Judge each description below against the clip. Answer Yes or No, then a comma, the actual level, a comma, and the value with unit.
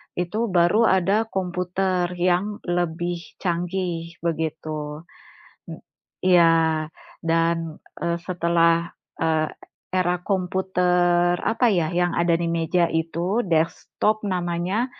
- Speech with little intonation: Yes, narrow, 1.7 semitones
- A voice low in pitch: No, medium, 175 Hz